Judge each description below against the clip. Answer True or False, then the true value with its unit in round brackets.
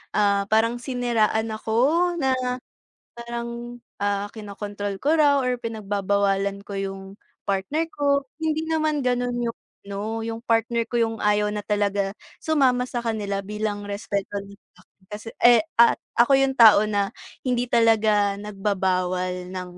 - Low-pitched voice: False (220 Hz)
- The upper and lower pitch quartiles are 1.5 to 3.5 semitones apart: True (3.2 semitones)